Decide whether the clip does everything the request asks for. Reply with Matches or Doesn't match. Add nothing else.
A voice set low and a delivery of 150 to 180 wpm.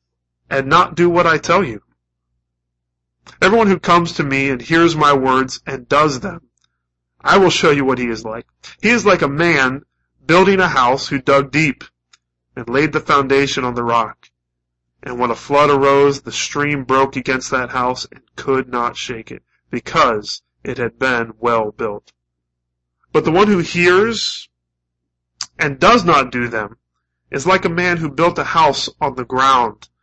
Matches